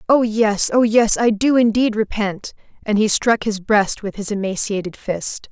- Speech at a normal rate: Yes, average, 185 wpm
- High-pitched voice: Yes, high, 215 Hz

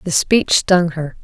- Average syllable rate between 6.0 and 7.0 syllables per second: No, 3.7 syllables/s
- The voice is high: No, medium, 175 Hz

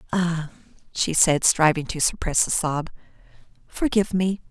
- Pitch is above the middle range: No, medium, 170 Hz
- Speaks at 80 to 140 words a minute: Yes, slow, 135 wpm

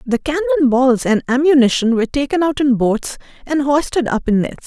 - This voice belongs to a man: No, female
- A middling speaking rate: Yes, average, 195 wpm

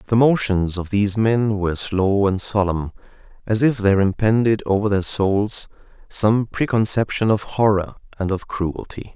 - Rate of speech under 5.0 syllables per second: Yes, 4.6 syllables/s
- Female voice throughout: No, male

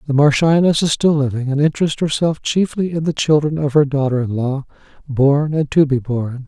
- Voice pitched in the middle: Yes, medium, 145 Hz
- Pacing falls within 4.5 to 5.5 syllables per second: Yes, 5.3 syllables/s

